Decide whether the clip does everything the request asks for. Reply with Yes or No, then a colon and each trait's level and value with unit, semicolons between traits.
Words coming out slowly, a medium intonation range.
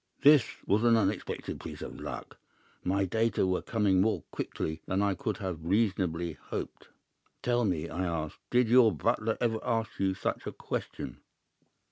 No: average, 160 wpm; average, 3.7 semitones